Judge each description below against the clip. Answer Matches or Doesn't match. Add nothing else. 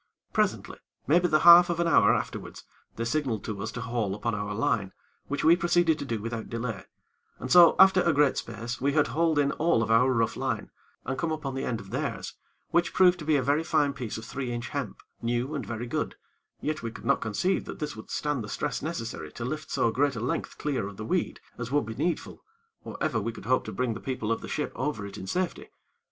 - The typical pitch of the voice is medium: Doesn't match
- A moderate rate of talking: Doesn't match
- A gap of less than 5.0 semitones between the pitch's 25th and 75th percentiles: Doesn't match